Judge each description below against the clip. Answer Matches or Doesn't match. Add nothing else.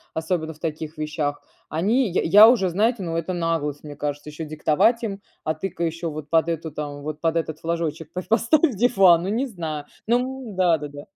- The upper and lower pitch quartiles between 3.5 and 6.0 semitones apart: Matches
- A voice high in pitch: Doesn't match